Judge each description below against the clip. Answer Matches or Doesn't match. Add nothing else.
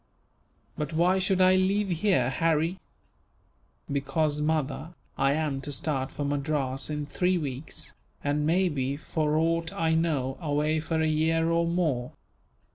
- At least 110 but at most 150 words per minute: Matches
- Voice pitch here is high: Doesn't match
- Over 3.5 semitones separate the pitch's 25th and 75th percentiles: Doesn't match